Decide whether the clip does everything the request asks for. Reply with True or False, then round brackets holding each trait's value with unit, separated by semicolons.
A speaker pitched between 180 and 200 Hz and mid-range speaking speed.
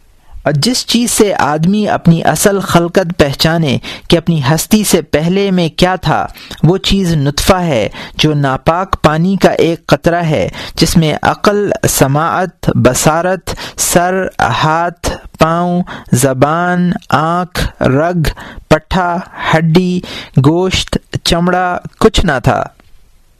False (170 Hz; 120 wpm)